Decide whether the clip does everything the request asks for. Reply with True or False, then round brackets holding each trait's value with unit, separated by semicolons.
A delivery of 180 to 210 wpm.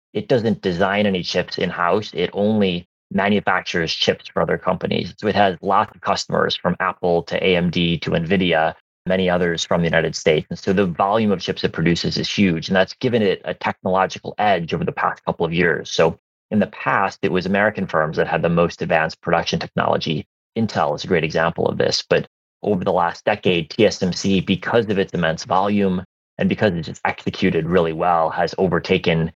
True (195 wpm)